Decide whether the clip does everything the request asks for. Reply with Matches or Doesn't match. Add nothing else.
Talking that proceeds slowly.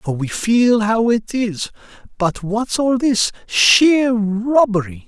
Matches